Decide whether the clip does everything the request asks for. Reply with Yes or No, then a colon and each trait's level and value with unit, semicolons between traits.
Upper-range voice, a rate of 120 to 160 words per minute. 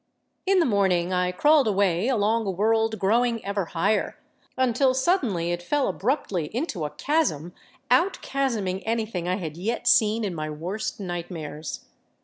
Yes: high, 205 Hz; average, 150 wpm